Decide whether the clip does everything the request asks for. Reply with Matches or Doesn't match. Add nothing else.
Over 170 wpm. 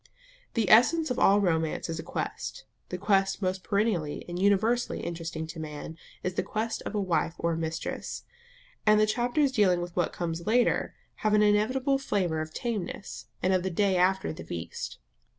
Matches